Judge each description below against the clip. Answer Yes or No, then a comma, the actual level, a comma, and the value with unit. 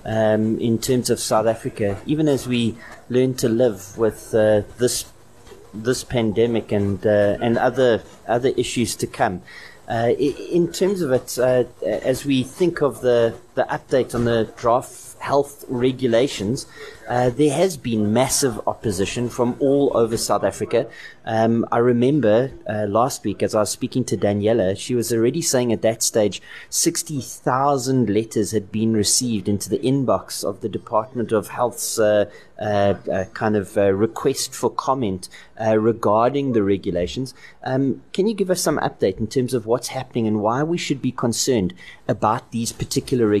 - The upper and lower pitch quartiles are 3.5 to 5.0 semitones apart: No, average, 3.1 semitones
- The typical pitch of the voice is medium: No, low, 120 Hz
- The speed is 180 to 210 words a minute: No, average, 165 wpm